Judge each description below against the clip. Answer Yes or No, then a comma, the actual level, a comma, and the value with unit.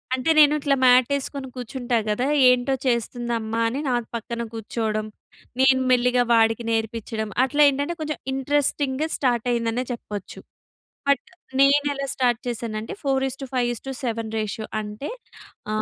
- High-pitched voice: Yes, high, 245 Hz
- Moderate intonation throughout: Yes, average, 3.0 semitones